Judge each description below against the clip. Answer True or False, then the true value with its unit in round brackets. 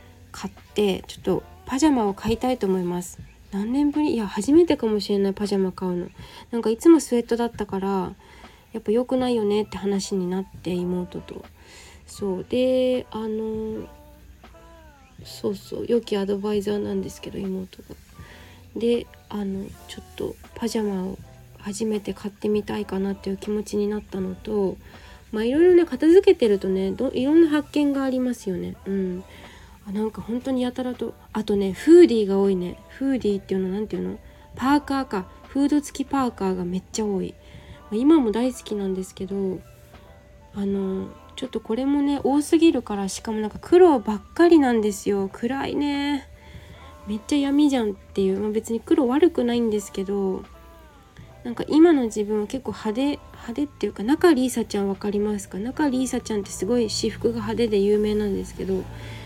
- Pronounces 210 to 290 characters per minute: False (365 characters per minute)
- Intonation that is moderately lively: True (4.7 semitones)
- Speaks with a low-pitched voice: False (210 Hz)